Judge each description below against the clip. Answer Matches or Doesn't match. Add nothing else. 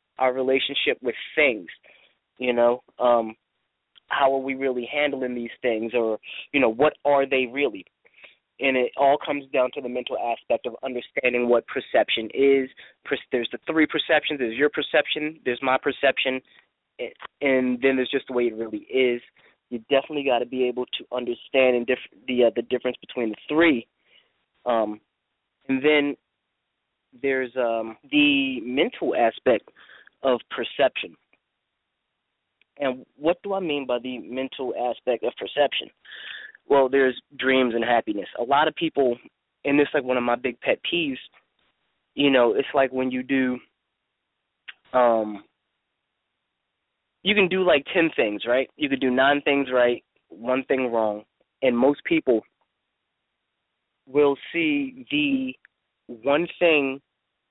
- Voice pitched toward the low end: Matches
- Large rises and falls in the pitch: Doesn't match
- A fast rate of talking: Doesn't match